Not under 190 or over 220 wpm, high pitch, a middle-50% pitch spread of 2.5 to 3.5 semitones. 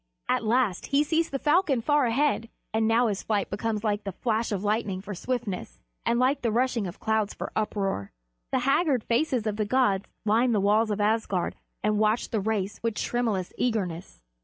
Yes: average, 195 wpm; high, 220 Hz; average, 3.2 semitones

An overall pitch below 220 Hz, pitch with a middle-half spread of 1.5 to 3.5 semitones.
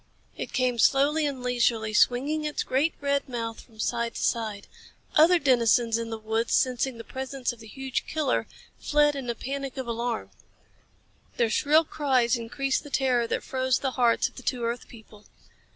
No: very high, 250 Hz; average, 2.9 semitones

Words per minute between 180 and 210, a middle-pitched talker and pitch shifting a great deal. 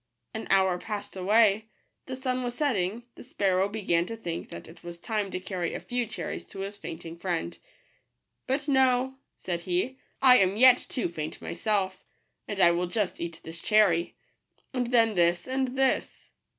No: average, 185 wpm; high, 200 Hz; wide, 5.9 semitones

